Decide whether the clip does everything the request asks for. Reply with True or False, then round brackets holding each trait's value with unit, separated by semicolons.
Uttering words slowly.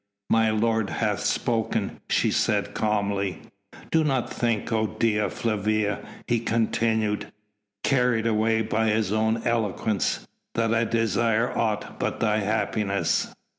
True (125 wpm)